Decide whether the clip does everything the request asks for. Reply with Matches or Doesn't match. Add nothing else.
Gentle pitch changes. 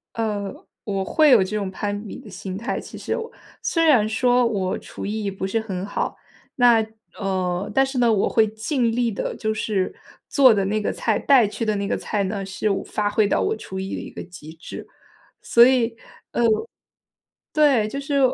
Doesn't match